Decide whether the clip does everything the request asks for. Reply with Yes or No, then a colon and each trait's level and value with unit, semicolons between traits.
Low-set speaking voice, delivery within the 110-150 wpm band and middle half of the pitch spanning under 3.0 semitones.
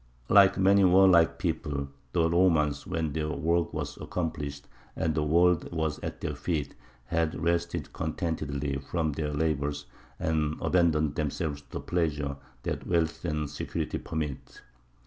Yes: very low, 80 Hz; average, 140 wpm; narrow, 2.6 semitones